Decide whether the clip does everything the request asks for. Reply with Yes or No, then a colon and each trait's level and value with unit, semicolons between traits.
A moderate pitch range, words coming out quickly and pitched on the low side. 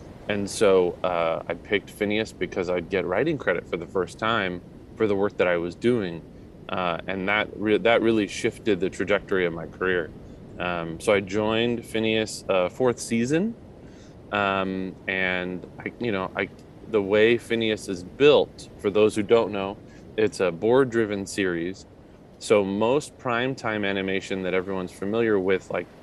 No: average, 3.3 semitones; average, 165 wpm; low, 100 Hz